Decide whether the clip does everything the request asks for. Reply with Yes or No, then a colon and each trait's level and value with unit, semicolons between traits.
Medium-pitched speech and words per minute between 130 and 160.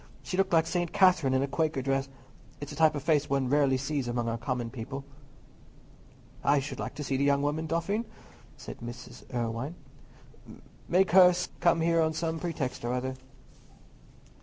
No: medium, 145 Hz; average, 175 wpm